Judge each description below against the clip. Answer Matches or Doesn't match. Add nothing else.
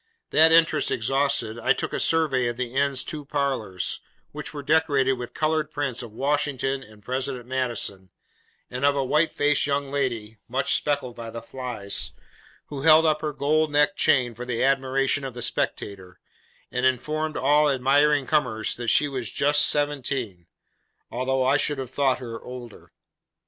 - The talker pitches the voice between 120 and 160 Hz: Matches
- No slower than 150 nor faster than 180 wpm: Matches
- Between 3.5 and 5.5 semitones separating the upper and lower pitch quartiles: Doesn't match